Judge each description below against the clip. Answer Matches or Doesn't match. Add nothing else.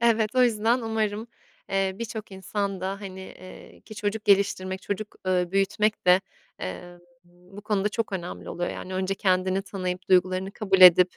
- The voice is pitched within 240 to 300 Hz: Doesn't match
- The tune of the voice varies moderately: Doesn't match